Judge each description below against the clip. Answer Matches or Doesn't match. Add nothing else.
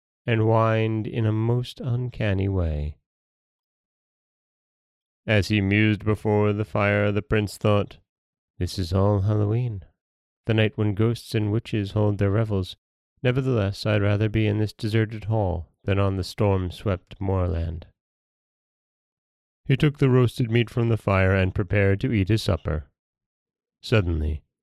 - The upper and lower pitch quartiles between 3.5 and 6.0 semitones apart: Doesn't match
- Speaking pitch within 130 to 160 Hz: Doesn't match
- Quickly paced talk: Doesn't match